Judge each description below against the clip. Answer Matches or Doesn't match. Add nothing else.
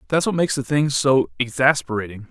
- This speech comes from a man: Matches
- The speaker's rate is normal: Matches